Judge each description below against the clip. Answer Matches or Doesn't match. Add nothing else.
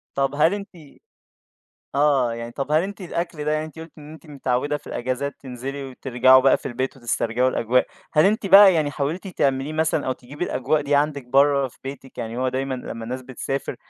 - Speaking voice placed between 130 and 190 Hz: Matches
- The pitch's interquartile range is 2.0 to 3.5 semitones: Matches